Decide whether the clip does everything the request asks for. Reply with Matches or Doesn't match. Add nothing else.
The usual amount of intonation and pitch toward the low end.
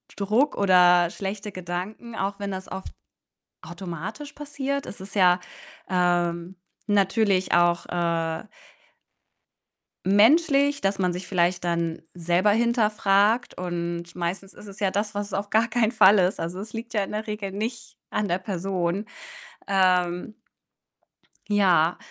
Doesn't match